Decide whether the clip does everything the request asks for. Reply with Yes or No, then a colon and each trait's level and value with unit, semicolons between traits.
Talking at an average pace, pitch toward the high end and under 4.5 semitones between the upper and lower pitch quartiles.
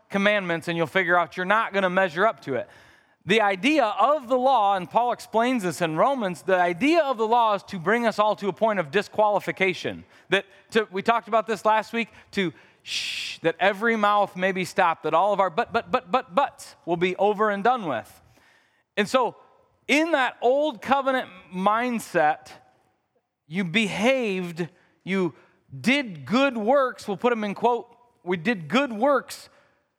No: average, 185 wpm; high, 210 Hz; average, 4.8 semitones